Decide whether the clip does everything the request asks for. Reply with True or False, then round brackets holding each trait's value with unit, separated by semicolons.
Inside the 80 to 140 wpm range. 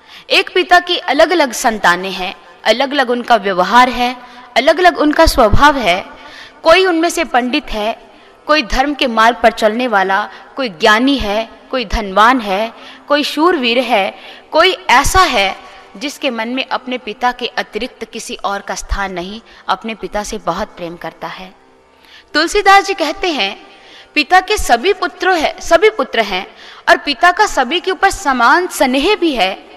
False (170 wpm)